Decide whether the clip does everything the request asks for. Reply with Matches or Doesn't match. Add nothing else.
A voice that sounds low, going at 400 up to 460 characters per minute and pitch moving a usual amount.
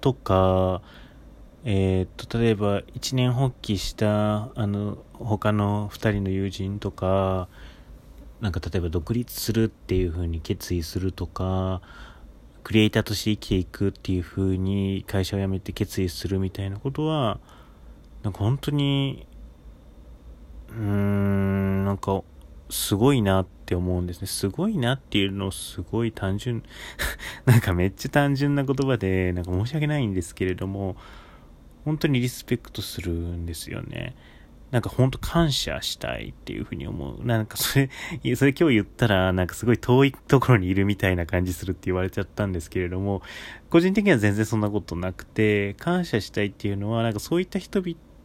Doesn't match